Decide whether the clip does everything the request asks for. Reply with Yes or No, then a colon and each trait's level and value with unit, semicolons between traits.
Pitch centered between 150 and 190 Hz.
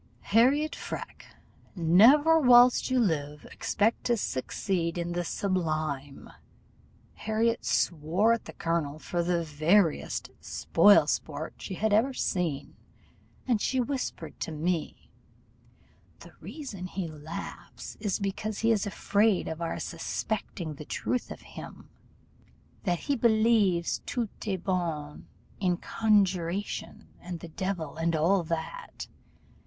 Yes: medium, 185 Hz